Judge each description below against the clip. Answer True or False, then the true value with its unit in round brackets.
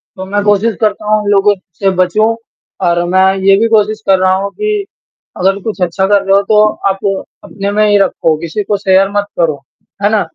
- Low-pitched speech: False (200 Hz)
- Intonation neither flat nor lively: False (1.9 semitones)